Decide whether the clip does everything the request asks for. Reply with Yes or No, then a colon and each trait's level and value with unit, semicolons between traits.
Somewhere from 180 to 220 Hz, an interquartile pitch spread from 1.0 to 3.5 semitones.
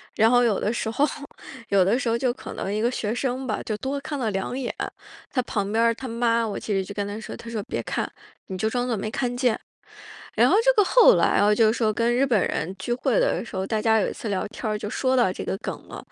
No: high, 230 Hz; average, 2.9 semitones